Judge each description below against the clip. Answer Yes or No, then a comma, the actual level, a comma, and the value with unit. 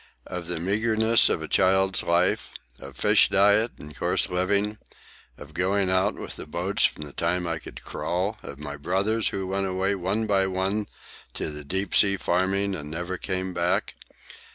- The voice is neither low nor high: No, very low, 95 Hz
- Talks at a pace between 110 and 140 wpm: No, average, 175 wpm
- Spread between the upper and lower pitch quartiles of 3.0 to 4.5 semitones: No, narrow, 2.4 semitones